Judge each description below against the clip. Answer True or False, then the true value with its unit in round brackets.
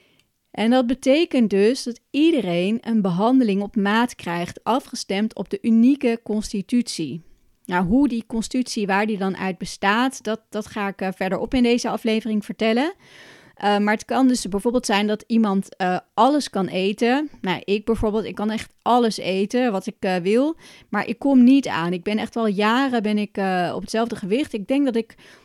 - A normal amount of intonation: True (3.4 semitones)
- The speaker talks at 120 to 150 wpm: False (185 wpm)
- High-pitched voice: True (220 Hz)